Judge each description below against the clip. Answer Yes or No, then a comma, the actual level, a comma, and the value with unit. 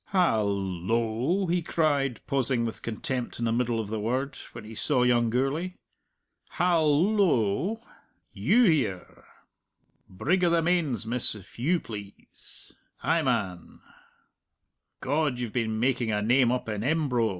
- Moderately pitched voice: No, low, 125 Hz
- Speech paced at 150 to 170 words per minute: No, average, 140 wpm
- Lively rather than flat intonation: Yes, wide, 6.1 semitones